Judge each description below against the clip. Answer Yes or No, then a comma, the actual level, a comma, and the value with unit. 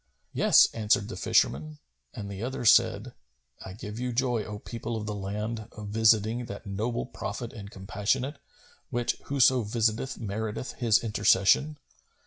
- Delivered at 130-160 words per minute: Yes, average, 145 wpm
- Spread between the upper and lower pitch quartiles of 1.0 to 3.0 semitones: Yes, narrow, 2.6 semitones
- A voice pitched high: No, low, 110 Hz